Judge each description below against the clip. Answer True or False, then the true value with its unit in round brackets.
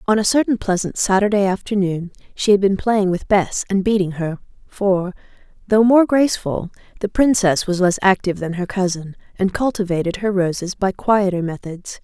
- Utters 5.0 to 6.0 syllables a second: True (5.2 syllables/s)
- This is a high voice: True (195 Hz)